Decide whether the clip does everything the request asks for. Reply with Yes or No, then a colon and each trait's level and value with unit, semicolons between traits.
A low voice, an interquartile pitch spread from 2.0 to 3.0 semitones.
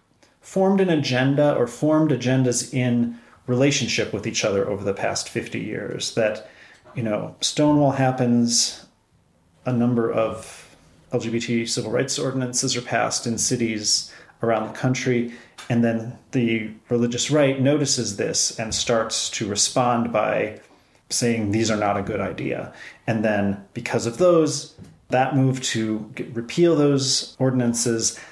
Yes: low, 120 Hz; average, 2.7 semitones